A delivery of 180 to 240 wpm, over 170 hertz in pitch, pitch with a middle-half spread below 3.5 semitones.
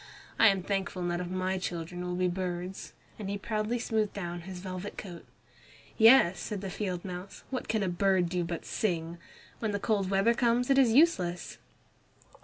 Yes: average, 185 wpm; high, 190 Hz; average, 3.1 semitones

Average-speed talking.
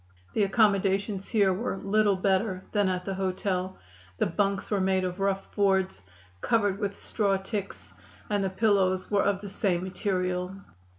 Yes: average, 160 wpm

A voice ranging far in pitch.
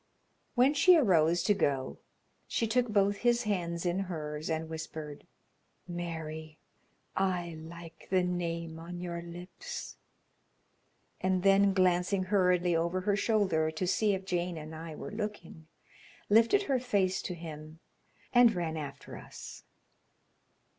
No: average, 3.6 semitones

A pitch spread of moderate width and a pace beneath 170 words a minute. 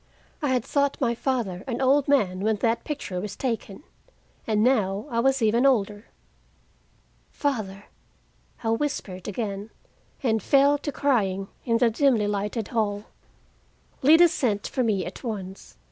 Yes: average, 4.7 semitones; average, 145 wpm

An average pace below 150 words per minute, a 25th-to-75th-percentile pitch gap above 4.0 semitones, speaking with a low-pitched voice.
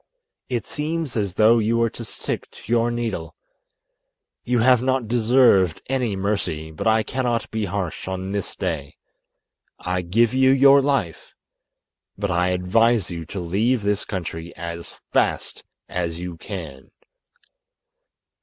Yes: average, 140 wpm; average, 5.0 semitones; low, 105 Hz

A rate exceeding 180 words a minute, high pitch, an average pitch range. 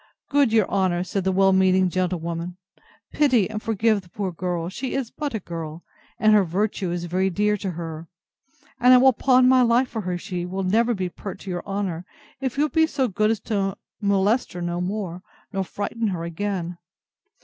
Yes: average, 200 wpm; high, 195 Hz; average, 4.0 semitones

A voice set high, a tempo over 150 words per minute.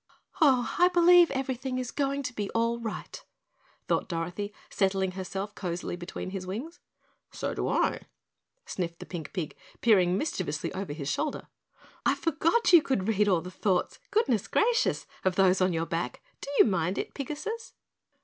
Yes: high, 205 Hz; average, 165 wpm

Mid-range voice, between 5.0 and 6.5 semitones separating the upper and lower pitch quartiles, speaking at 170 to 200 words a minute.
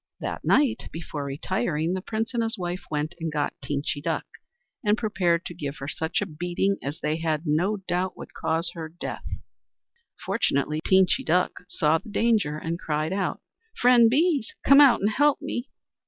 Yes: medium, 175 Hz; wide, 5.5 semitones; average, 175 wpm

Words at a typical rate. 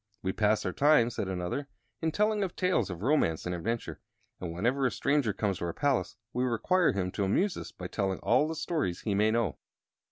No: fast, 215 wpm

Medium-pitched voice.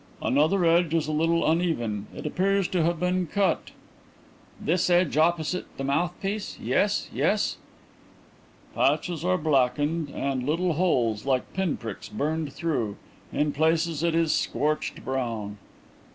Yes: medium, 160 Hz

